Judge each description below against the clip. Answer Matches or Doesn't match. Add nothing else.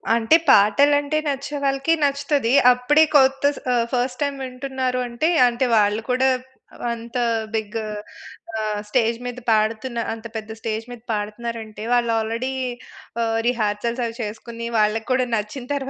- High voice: Matches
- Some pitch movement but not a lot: Matches